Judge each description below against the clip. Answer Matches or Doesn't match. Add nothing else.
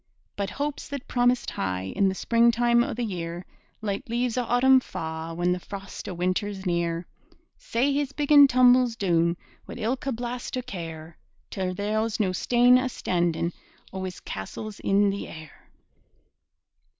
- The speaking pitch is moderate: Doesn't match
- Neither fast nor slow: Matches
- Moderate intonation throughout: Doesn't match